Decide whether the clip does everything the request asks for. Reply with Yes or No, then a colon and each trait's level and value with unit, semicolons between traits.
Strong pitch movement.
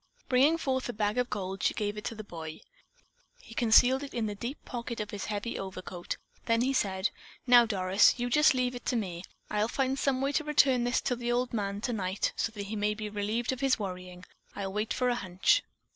No: average, 3.7 semitones